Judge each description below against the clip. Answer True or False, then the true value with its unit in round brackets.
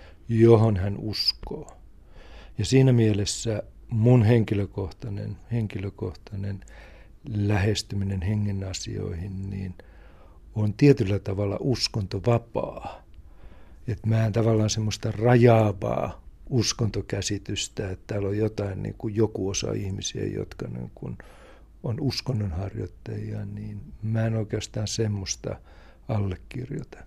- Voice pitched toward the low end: True (105 Hz)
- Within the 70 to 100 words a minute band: True (95 wpm)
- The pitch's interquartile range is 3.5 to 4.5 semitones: False (2.4 semitones)